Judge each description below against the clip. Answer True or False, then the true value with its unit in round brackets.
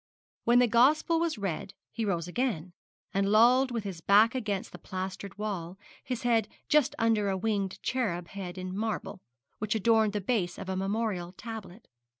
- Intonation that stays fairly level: False (3.5 semitones)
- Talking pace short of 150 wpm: False (170 wpm)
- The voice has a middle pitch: False (210 Hz)